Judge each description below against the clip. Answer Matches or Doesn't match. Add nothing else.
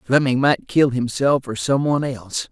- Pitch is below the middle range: Matches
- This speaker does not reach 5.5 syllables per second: Matches